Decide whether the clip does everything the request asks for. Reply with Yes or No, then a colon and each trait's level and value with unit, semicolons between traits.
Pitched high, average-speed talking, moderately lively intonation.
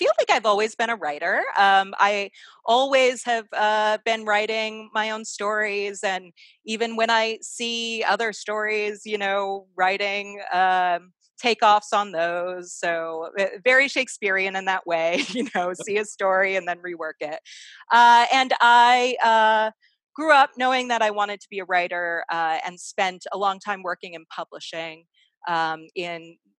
Yes: high, 205 Hz; average, 160 wpm; average, 3.9 semitones